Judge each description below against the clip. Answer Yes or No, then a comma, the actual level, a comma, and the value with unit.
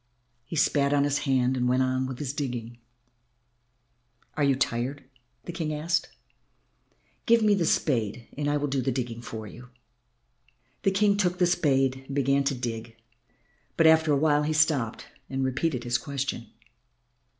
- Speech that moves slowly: No, average, 165 wpm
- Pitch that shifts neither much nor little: Yes, average, 3.5 semitones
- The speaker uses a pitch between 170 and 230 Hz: No, low, 135 Hz